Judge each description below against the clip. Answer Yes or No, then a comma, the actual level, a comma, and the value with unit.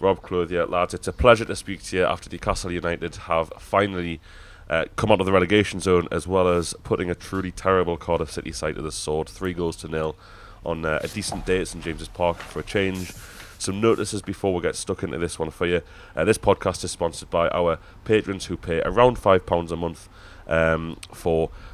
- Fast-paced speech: Yes, fast, 220 wpm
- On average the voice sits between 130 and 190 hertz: No, very low, 90 Hz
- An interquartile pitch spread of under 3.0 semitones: Yes, narrow, 2.4 semitones